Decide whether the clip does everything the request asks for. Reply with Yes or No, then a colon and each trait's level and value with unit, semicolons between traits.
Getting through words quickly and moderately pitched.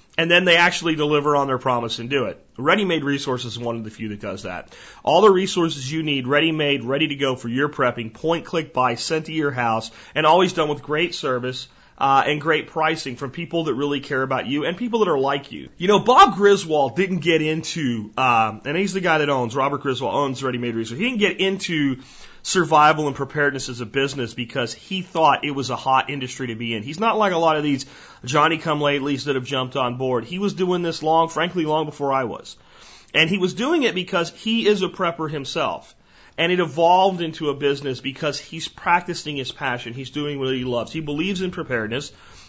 Yes: fast, 225 wpm; medium, 150 Hz